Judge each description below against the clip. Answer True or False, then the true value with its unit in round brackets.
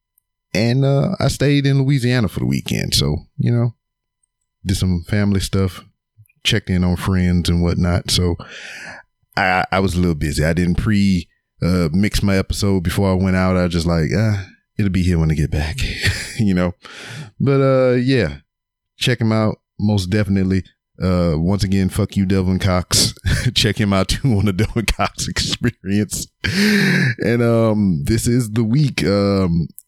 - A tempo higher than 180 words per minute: False (170 wpm)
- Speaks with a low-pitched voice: True (100 Hz)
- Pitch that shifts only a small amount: False (4.6 semitones)